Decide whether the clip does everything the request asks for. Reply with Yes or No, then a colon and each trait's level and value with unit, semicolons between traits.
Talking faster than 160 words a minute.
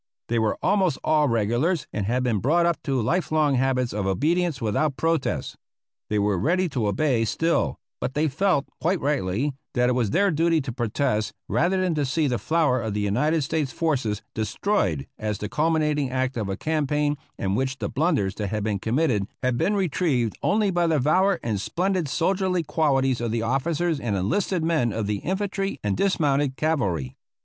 Yes: average, 190 wpm